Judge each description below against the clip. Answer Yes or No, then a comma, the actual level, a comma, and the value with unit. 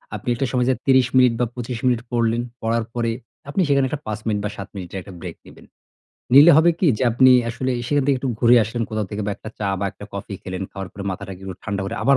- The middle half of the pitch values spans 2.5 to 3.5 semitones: No, average, 4.2 semitones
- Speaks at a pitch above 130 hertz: No, low, 115 Hz